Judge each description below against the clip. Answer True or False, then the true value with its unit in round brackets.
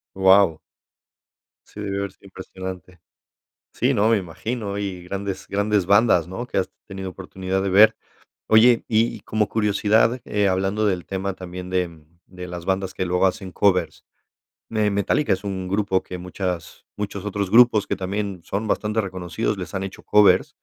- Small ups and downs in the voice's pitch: True (2.1 semitones)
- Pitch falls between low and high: False (95 Hz)